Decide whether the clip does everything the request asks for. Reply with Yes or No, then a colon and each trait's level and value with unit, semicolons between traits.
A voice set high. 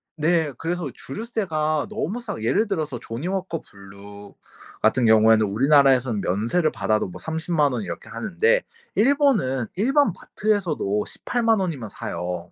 No: medium, 155 Hz